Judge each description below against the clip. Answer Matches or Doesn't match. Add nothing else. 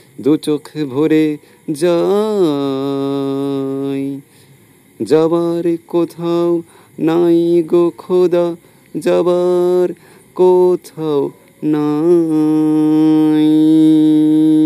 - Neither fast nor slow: Matches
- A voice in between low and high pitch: Matches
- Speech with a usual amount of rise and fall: Doesn't match